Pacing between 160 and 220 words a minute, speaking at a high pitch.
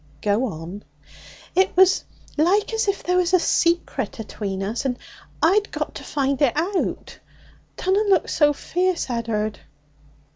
No: average, 145 wpm; very high, 310 Hz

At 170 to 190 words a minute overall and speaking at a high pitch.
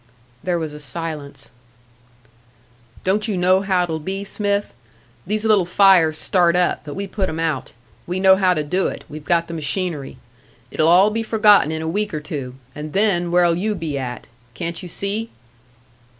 No: average, 180 wpm; medium, 175 Hz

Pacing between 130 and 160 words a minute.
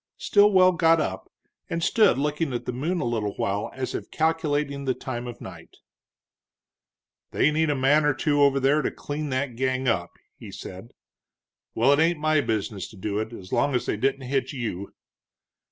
No: average, 185 wpm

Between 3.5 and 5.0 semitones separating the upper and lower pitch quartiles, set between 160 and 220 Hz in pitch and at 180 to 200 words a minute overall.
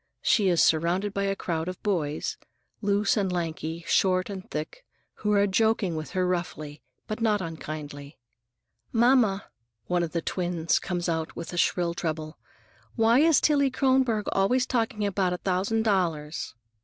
No: average, 4.1 semitones; medium, 185 Hz; average, 150 wpm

